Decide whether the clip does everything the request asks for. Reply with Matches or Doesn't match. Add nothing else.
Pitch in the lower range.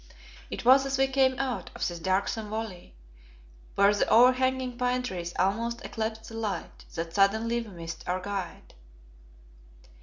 Doesn't match